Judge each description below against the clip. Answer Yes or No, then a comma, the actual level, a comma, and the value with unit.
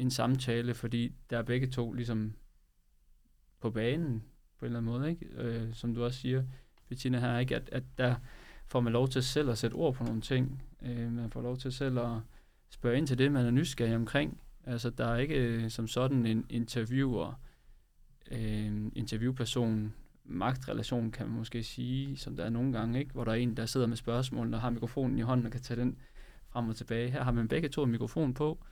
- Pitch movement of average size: No, narrow, 2.0 semitones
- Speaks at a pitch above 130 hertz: No, low, 120 Hz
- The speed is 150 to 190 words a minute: No, average, 210 wpm